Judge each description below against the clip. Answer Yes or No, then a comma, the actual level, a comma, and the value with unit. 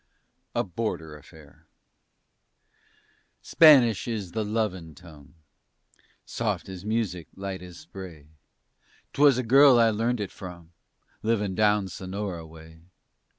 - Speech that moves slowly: Yes, slow, 110 wpm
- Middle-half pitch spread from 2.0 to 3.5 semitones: No, average, 5.0 semitones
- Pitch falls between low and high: No, very low, 95 Hz